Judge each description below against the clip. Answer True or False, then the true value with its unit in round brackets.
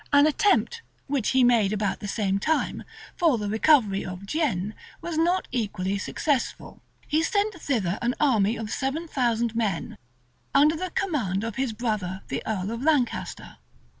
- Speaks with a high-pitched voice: True (235 Hz)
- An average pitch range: False (6.8 semitones)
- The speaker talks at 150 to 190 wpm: True (160 wpm)